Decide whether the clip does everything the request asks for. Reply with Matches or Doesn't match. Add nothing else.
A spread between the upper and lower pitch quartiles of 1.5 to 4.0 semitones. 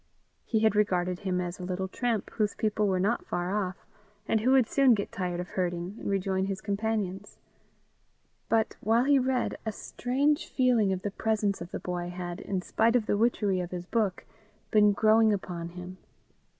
Matches